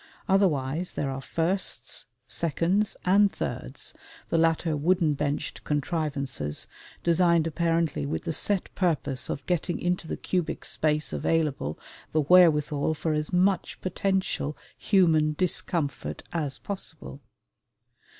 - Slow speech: Yes, slow, 115 wpm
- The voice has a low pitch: No, medium, 165 Hz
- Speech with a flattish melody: No, average, 3.3 semitones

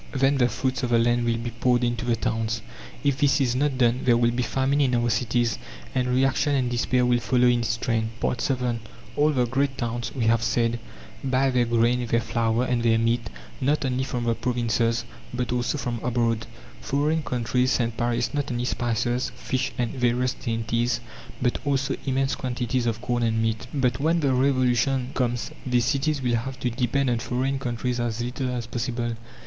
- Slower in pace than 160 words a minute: No, average, 195 wpm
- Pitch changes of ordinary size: No, narrow, 1.7 semitones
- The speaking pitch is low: Yes, low, 125 Hz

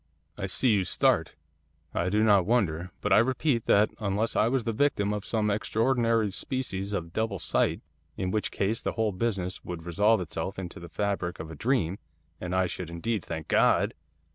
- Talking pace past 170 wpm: Yes, average, 190 wpm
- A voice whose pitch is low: Yes, low, 100 Hz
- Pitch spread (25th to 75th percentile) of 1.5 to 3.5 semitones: No, average, 3.9 semitones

